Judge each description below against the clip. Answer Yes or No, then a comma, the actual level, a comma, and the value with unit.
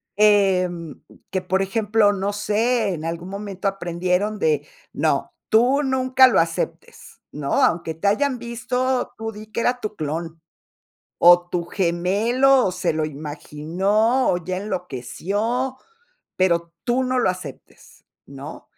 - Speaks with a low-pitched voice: No, high, 195 Hz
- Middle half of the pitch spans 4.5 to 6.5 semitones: Yes, average, 4.9 semitones